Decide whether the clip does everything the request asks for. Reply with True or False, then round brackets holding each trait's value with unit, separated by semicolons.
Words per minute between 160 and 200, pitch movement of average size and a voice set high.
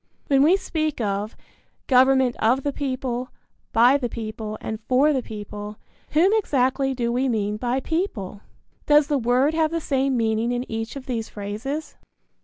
True (165 wpm; 4.0 semitones; 255 Hz)